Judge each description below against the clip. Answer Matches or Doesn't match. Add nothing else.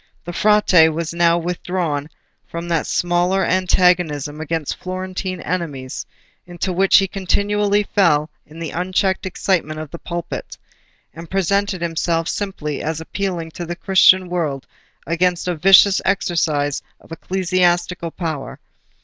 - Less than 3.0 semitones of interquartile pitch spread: Matches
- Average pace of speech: Doesn't match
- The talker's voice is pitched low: Doesn't match